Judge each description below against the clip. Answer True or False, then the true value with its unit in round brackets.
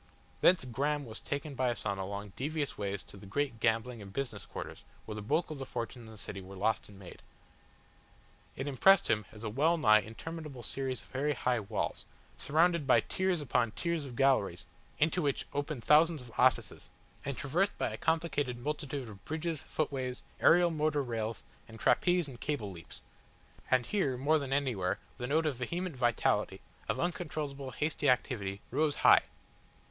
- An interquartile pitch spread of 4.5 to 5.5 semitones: True (5.2 semitones)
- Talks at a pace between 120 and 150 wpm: False (175 wpm)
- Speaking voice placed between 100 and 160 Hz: True (135 Hz)